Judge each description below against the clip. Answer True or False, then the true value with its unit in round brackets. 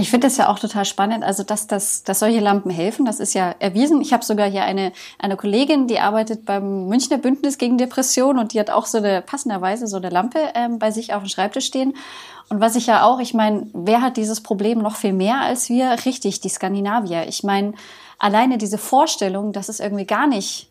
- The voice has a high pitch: True (215 Hz)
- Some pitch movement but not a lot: True (3.8 semitones)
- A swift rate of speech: True (225 wpm)